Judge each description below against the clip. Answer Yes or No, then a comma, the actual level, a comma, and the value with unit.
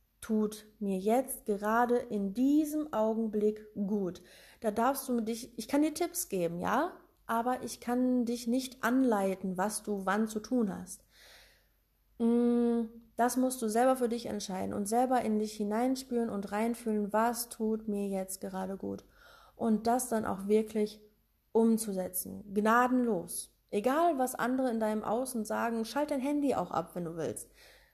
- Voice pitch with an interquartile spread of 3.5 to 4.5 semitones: No, average, 2.9 semitones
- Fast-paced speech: No, average, 155 wpm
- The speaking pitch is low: No, high, 225 Hz